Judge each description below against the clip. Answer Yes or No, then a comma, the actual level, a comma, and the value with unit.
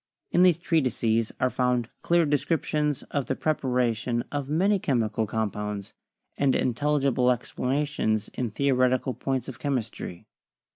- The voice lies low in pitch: Yes, low, 130 Hz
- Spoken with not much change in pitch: No, average, 3.8 semitones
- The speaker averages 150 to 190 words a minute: No, slow, 135 wpm